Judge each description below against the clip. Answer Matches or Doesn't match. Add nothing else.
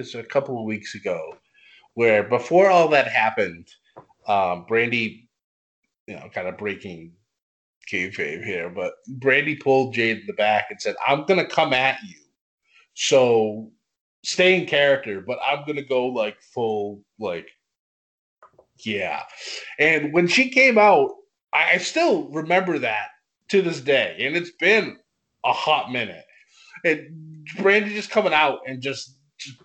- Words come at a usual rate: Matches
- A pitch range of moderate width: Doesn't match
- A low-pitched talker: Doesn't match